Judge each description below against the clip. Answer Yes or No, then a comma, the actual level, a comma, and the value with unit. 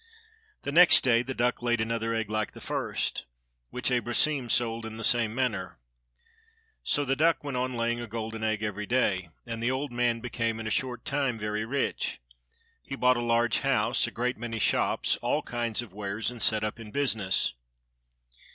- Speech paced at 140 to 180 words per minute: No, average, 190 wpm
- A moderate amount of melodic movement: No, narrow, 2.2 semitones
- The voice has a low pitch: Yes, low, 115 Hz